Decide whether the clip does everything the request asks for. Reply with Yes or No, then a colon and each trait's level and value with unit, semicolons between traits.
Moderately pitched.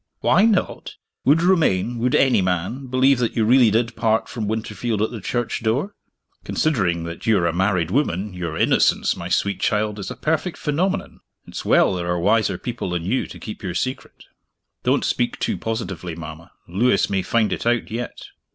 No: low, 110 Hz